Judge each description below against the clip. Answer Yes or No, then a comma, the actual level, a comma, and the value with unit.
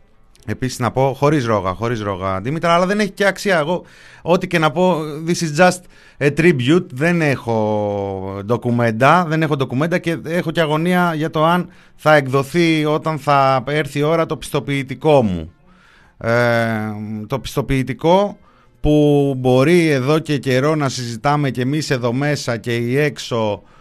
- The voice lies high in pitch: No, medium, 145 Hz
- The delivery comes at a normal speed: Yes, average, 160 wpm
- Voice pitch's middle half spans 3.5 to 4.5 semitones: No, average, 5.1 semitones